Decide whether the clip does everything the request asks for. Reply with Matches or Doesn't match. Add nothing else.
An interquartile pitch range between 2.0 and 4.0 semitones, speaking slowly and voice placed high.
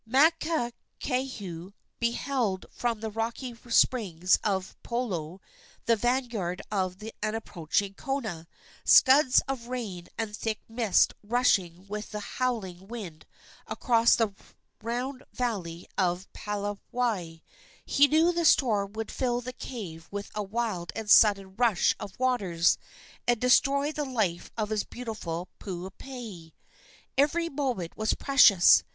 Doesn't match